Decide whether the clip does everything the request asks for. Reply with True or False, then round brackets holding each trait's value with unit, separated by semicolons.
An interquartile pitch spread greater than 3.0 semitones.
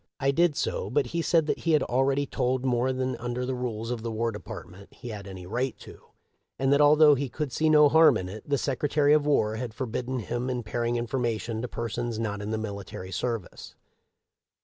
True (3.9 semitones)